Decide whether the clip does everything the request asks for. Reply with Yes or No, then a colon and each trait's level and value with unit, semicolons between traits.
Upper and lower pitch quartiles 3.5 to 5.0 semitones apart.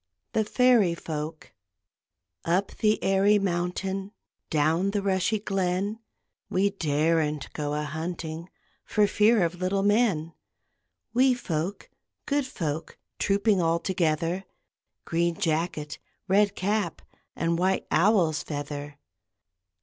Yes: average, 4.0 semitones